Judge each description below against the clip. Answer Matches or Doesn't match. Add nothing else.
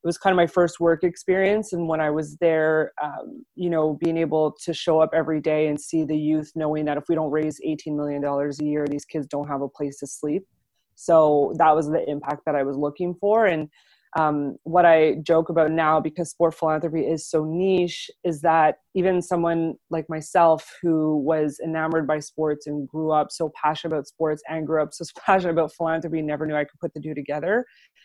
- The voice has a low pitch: Doesn't match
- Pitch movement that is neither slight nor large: Doesn't match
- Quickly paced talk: Matches